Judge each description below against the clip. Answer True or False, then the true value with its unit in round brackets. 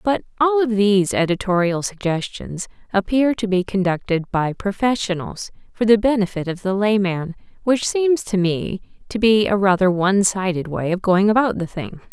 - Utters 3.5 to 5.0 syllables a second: True (4.9 syllables/s)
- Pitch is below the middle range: False (200 Hz)